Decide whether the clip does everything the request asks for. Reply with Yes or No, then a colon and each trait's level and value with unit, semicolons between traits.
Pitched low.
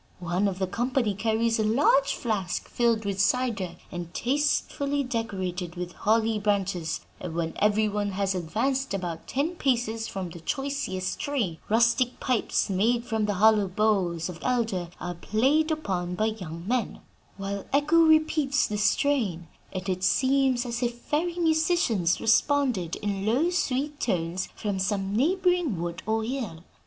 No: high, 220 Hz